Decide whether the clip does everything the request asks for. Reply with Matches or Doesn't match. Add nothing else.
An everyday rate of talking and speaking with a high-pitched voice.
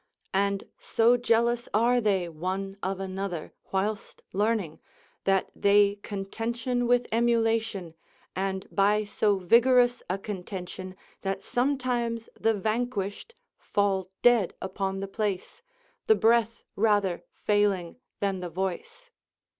Doesn't match